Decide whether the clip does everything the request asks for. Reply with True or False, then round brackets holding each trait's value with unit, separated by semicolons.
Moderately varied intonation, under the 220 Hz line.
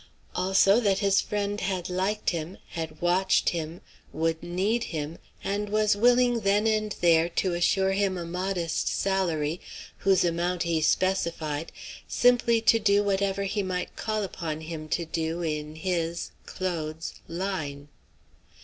True (3.4 semitones; 185 Hz)